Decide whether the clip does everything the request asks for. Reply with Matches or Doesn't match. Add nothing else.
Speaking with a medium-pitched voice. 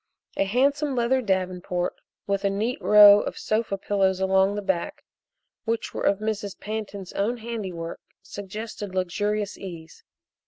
Doesn't match